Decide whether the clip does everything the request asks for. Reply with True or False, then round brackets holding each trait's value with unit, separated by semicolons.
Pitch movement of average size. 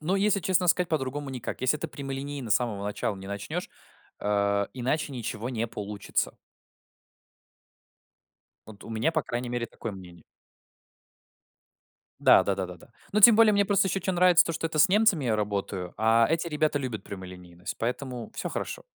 False (7.9 semitones)